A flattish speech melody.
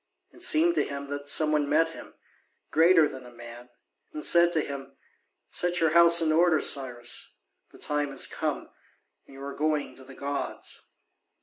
No: average, 3.0 semitones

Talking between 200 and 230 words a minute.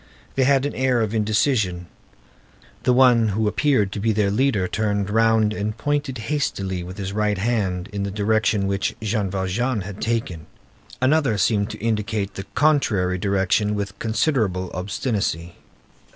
No: average, 150 wpm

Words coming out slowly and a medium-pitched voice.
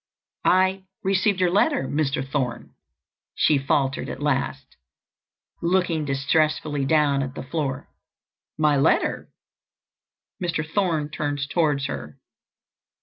Yes: slow, 100 wpm; medium, 150 Hz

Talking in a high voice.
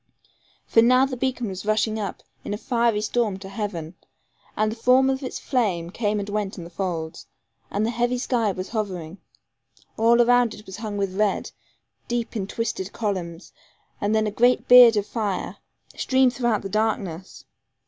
Yes: high, 215 Hz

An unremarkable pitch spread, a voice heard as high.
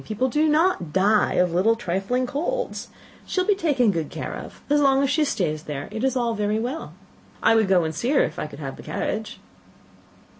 No: wide, 7.4 semitones; high, 225 Hz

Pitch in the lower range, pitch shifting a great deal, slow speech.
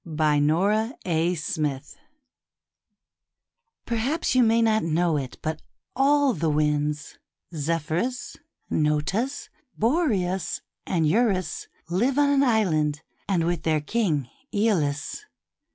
No: medium, 180 Hz; wide, 7.5 semitones; slow, 95 wpm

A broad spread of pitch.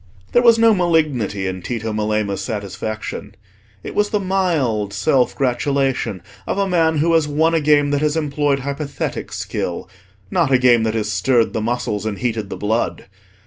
Yes: wide, 6.7 semitones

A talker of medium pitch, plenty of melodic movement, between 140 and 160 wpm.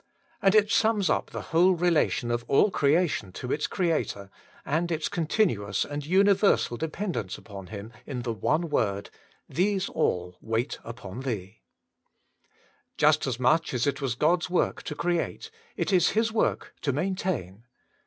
Yes: medium, 150 Hz; wide, 7.6 semitones; average, 155 wpm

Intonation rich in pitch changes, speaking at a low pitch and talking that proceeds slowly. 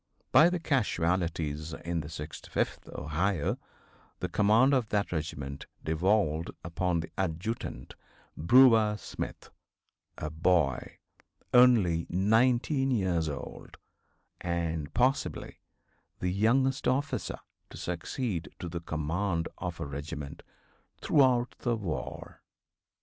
Yes: wide, 6.6 semitones; very low, 90 Hz; slow, 105 wpm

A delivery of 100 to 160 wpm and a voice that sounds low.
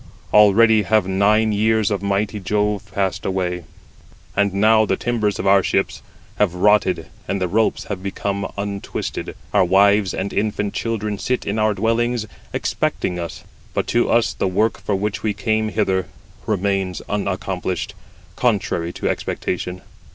Yes: average, 150 wpm; low, 100 Hz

